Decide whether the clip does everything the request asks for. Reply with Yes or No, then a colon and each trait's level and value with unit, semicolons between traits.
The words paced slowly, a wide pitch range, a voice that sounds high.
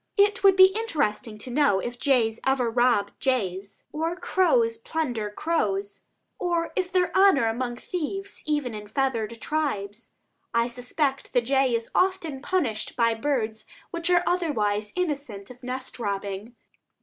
No: average, 150 wpm; wide, 7.1 semitones; very high, 255 Hz